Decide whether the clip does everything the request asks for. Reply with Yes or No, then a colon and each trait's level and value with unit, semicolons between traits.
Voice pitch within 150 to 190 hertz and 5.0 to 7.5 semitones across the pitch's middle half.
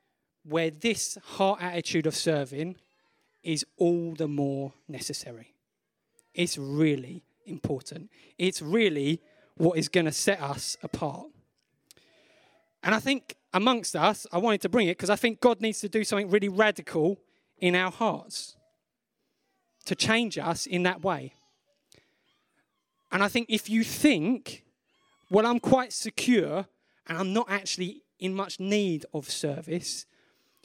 Yes: medium, 185 Hz; wide, 5.4 semitones